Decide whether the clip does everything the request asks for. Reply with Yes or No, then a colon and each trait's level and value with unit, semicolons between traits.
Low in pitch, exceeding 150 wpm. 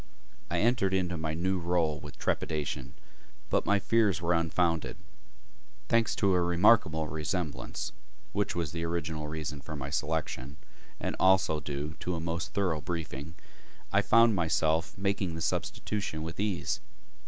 No: very low, 85 Hz; average, 145 wpm